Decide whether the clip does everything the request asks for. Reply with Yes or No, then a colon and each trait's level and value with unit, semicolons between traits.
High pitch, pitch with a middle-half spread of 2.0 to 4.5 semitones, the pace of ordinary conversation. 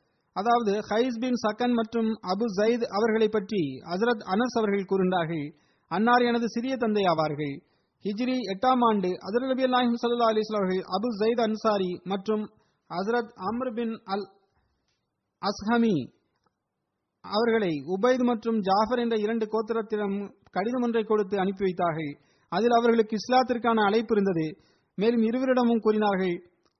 Yes: high, 220 Hz; average, 3.5 semitones; average, 110 wpm